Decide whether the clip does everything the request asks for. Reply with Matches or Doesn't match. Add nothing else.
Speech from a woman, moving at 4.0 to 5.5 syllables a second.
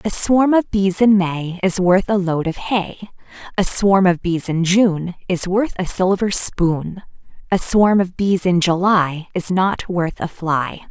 Doesn't match